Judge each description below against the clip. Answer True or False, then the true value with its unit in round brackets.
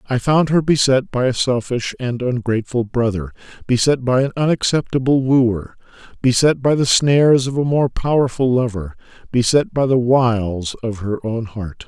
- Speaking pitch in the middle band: False (125 Hz)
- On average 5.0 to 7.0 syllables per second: False (4.8 syllables/s)